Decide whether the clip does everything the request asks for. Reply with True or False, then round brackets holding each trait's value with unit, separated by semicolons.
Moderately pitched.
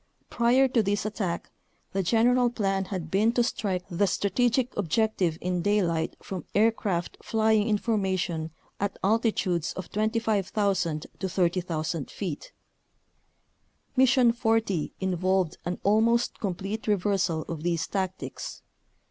False (195 Hz)